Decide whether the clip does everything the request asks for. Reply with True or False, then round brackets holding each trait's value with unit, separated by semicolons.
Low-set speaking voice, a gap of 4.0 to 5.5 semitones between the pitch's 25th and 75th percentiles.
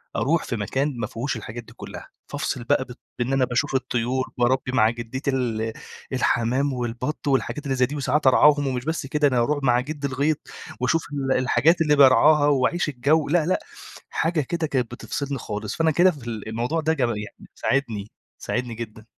False (130 Hz; 3.6 semitones)